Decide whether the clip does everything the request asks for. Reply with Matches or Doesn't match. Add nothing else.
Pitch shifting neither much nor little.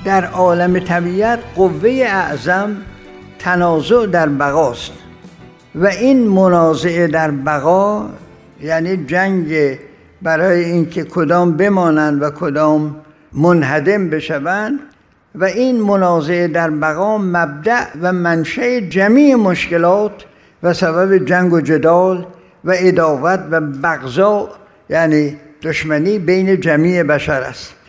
Matches